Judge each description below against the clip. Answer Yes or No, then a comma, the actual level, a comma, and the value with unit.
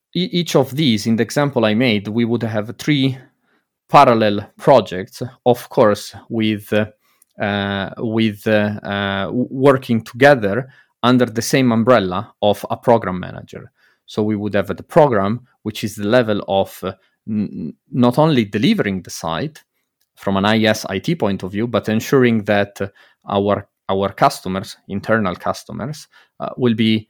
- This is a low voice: Yes, low, 110 Hz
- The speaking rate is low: No, average, 155 wpm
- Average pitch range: Yes, average, 3.7 semitones